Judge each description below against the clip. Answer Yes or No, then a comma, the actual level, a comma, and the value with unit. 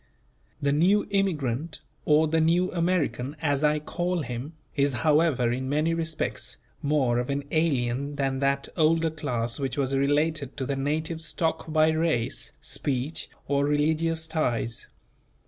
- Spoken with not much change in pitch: No, average, 3.1 semitones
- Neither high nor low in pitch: Yes, medium, 150 Hz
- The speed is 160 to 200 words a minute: No, average, 145 wpm